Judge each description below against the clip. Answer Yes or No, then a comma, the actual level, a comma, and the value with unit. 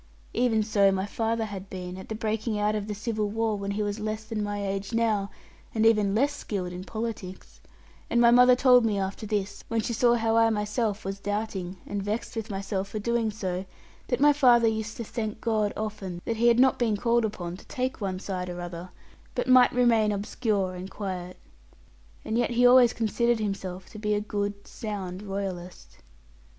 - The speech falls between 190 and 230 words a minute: Yes, average, 200 wpm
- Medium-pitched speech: No, high, 210 Hz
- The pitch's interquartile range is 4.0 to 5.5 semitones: No, narrow, 2.6 semitones